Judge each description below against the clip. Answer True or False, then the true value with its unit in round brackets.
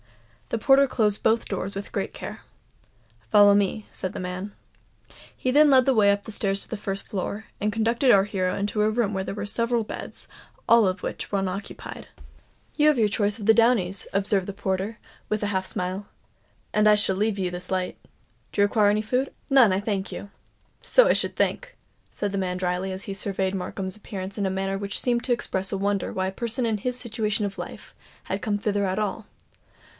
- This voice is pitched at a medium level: False (205 Hz)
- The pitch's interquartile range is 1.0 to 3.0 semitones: True (2.5 semitones)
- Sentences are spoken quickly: True (210 wpm)